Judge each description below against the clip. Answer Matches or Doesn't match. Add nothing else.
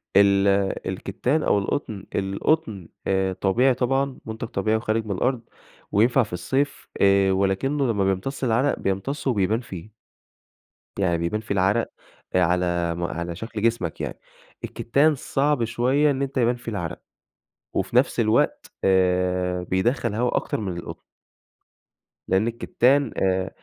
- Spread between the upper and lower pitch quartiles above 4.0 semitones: Matches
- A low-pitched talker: Matches